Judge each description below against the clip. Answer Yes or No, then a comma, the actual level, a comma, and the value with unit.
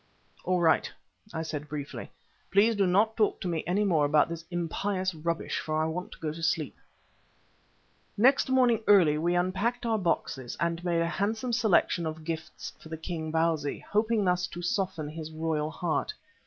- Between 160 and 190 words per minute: Yes, average, 180 wpm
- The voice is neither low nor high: Yes, medium, 170 Hz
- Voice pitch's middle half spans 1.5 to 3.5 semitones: No, average, 3.9 semitones